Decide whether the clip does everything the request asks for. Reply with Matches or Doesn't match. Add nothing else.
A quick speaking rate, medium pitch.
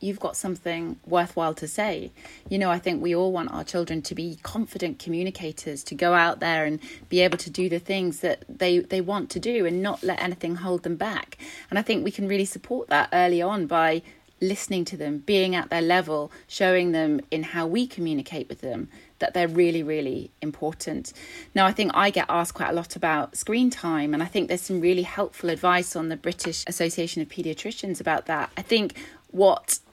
Matches